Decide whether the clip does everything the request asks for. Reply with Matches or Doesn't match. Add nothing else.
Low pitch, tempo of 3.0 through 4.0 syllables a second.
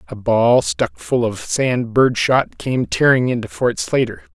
Matches